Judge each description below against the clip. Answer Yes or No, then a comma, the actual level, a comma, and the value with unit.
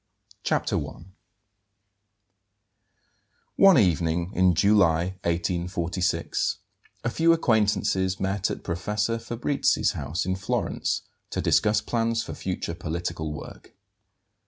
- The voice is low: Yes, very low, 95 Hz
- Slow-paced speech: Yes, slow, 100 wpm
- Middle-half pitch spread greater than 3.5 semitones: Yes, average, 4.0 semitones